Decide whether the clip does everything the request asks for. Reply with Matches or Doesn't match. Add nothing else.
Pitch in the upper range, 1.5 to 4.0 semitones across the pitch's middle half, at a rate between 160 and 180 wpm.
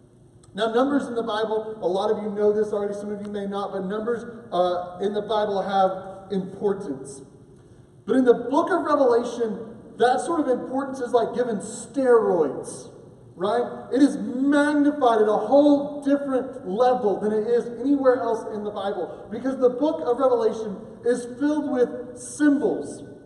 Matches